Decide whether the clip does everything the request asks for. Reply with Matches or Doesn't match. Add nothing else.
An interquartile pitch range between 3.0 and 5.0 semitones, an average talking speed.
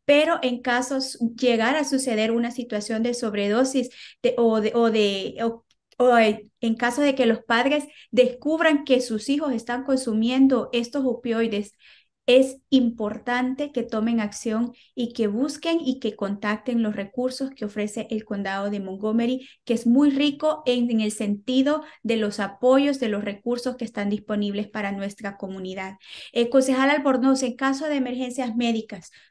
Matches